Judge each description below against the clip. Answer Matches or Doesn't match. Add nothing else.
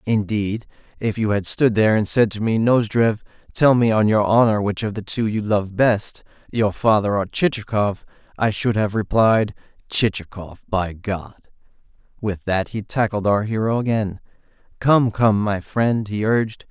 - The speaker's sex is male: Matches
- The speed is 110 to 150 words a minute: Doesn't match